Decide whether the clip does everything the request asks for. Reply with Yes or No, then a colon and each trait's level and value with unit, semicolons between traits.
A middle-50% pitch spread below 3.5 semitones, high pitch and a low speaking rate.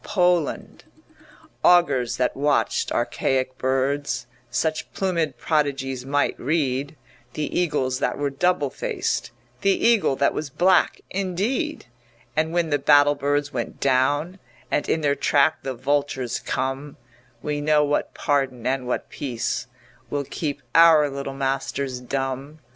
No: average, 2.9 semitones; medium, 145 Hz; slow, 130 wpm